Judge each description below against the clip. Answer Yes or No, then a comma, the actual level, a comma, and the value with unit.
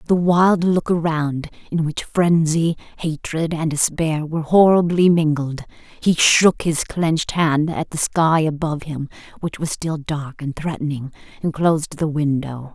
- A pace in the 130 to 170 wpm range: Yes, average, 160 wpm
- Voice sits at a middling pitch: Yes, medium, 160 Hz